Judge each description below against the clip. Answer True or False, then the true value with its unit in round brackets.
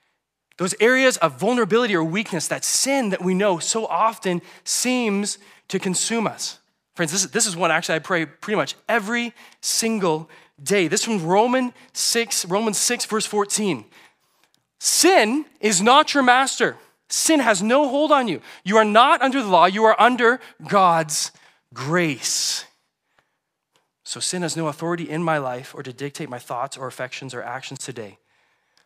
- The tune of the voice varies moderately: False (6.2 semitones)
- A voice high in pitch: True (205 Hz)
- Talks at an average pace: True (160 wpm)